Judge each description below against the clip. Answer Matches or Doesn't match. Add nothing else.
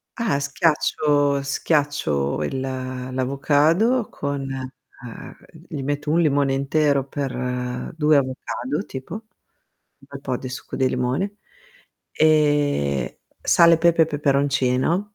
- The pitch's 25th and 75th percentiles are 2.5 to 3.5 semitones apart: Matches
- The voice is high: Doesn't match